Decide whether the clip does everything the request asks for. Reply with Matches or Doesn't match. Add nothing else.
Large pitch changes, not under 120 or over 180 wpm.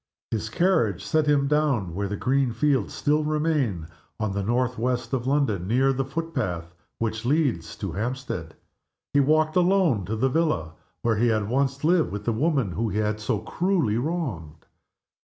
Matches